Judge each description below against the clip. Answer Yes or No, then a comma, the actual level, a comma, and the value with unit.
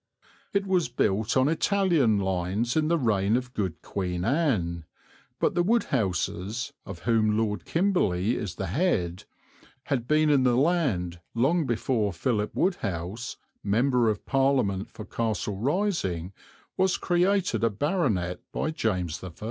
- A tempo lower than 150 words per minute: Yes, average, 140 wpm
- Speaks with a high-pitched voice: No, low, 115 Hz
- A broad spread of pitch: Yes, wide, 7.9 semitones